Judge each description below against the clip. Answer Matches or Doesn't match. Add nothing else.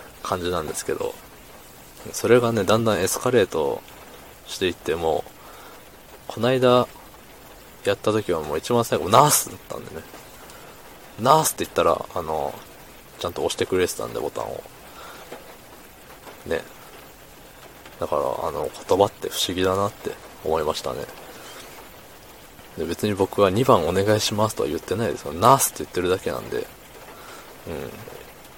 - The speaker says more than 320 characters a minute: Doesn't match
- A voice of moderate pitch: Doesn't match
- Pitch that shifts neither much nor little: Matches